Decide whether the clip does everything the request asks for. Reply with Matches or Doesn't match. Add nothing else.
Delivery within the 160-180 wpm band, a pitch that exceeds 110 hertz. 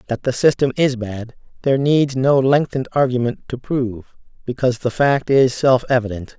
Matches